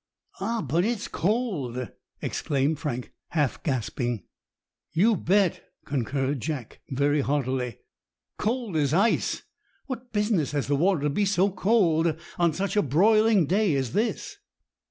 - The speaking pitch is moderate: Yes, medium, 160 Hz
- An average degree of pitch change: No, wide, 6.8 semitones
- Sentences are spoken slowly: Yes, slow, 130 wpm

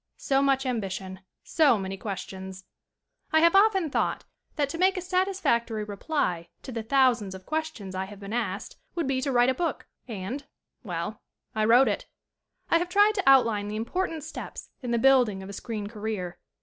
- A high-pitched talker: Yes, high, 235 Hz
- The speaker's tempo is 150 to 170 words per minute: No, average, 190 wpm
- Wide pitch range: Yes, wide, 7.4 semitones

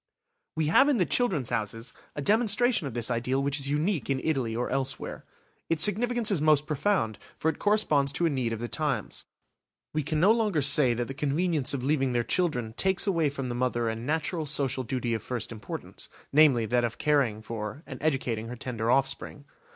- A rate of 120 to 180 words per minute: No, average, 200 wpm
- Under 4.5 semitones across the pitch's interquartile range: No, average, 4.9 semitones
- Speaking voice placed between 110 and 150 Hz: Yes, medium, 140 Hz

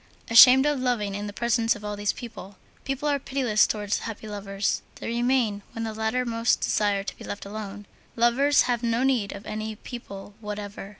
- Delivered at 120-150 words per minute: No, average, 190 wpm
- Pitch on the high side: Yes, high, 220 Hz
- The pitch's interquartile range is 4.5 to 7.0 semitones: No, average, 3.0 semitones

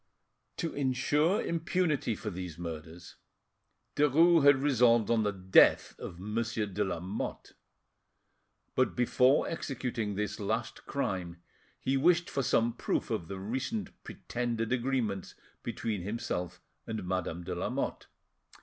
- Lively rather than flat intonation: Yes, wide, 6.1 semitones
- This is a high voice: No, low, 115 Hz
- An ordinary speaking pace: No, slow, 120 wpm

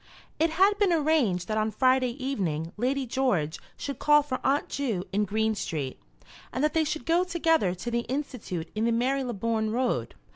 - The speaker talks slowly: No, average, 180 wpm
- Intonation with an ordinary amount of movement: No, wide, 5.9 semitones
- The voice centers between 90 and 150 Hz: No, very high, 250 Hz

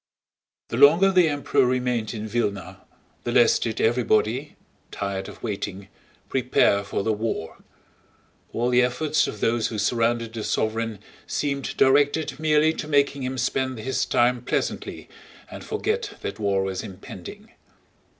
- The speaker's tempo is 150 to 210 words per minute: No, slow, 135 wpm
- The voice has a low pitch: Yes, low, 120 Hz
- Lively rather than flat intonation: No, average, 4.3 semitones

